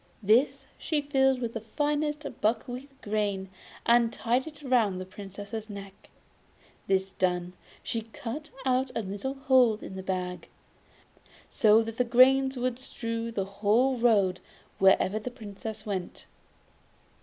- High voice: Yes, high, 225 Hz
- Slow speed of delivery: Yes, slow, 130 wpm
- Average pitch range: Yes, average, 4.4 semitones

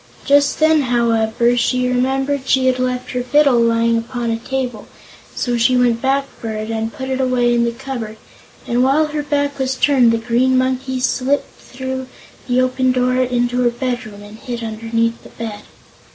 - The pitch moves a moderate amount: No, narrow, 2.0 semitones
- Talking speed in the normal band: Yes, average, 180 wpm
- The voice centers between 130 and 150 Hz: No, very high, 250 Hz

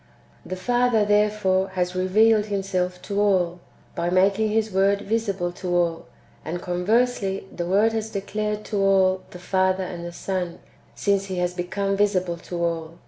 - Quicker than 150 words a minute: Yes, average, 160 wpm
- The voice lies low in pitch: No, high, 190 Hz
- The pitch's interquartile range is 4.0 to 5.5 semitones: No, narrow, 2.5 semitones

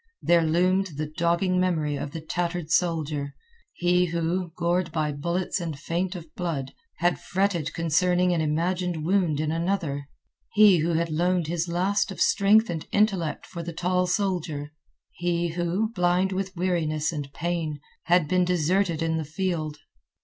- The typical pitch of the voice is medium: Yes, medium, 170 Hz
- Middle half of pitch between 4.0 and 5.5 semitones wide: No, narrow, 2.4 semitones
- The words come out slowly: No, average, 155 wpm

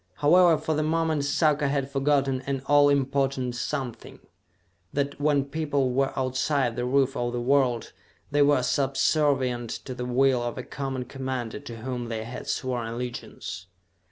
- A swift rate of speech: No, average, 155 wpm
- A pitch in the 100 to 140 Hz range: Yes, low, 135 Hz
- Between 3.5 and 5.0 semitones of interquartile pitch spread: No, narrow, 2.4 semitones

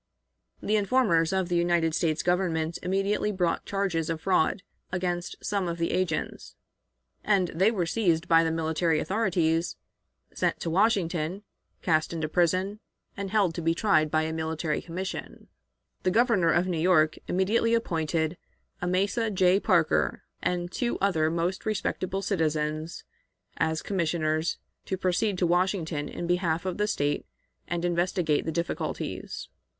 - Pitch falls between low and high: Yes, medium, 175 Hz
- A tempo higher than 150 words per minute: No, average, 145 wpm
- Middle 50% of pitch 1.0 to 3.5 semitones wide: Yes, average, 2.9 semitones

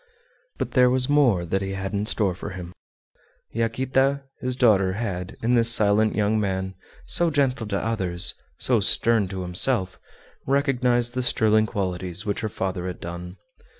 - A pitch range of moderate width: Yes, average, 4.7 semitones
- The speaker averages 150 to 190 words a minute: Yes, average, 160 wpm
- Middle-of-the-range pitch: No, low, 105 Hz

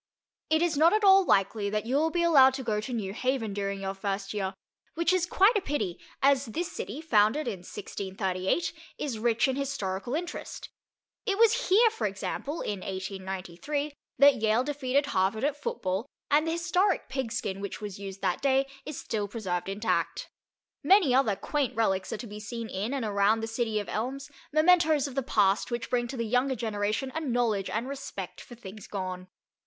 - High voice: Yes, high, 235 Hz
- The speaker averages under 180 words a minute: No, average, 190 wpm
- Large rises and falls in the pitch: Yes, wide, 6.2 semitones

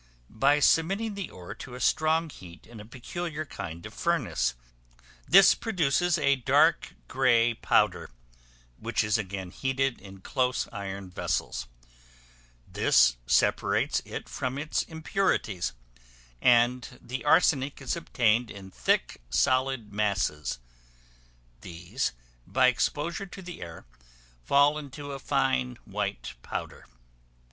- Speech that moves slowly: Yes, slow, 120 wpm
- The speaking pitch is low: Yes, low, 130 Hz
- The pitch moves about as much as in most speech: No, wide, 6.5 semitones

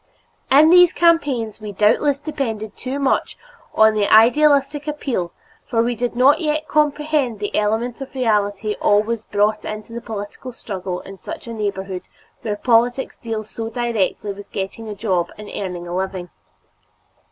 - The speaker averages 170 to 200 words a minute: No, average, 155 wpm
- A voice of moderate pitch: No, high, 225 Hz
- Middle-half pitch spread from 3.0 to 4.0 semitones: No, average, 4.5 semitones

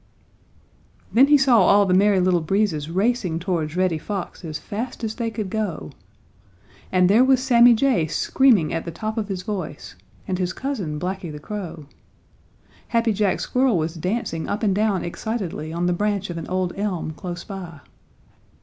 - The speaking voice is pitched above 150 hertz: Yes, high, 190 Hz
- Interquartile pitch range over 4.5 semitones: No, average, 4.2 semitones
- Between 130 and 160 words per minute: No, average, 175 wpm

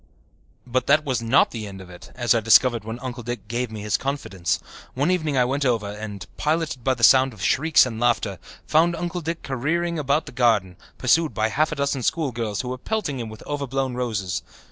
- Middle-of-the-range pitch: No, low, 125 Hz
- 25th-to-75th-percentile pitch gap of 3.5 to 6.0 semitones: Yes, average, 4.6 semitones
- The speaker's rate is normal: No, fast, 210 wpm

